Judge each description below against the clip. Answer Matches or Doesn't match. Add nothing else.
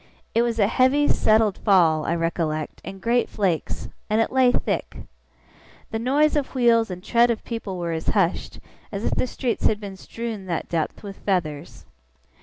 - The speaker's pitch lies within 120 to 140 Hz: Doesn't match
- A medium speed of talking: Matches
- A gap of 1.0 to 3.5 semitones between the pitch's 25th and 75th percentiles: Doesn't match